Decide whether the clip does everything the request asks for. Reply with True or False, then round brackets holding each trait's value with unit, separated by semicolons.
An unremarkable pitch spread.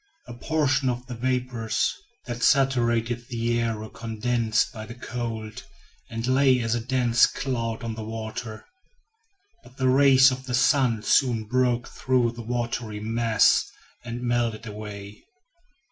False (2.0 semitones)